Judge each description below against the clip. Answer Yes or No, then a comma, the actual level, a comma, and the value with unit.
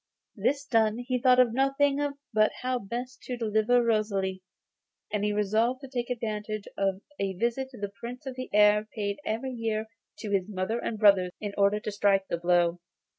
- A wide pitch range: No, average, 3.6 semitones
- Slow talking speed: No, average, 185 wpm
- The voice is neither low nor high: No, high, 215 Hz